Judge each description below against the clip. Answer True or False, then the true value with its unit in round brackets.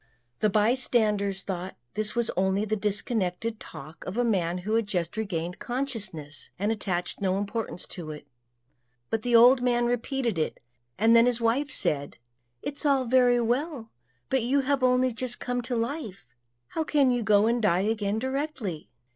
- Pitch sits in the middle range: False (225 Hz)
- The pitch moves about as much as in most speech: True (4.1 semitones)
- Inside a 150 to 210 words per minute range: True (170 wpm)